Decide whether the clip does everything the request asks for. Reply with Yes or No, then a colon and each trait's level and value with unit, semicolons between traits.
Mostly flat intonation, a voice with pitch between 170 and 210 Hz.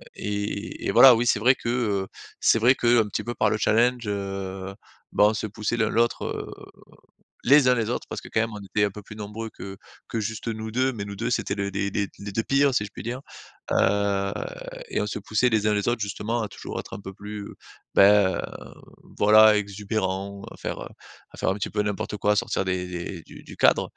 No: narrow, 2.3 semitones; low, 105 Hz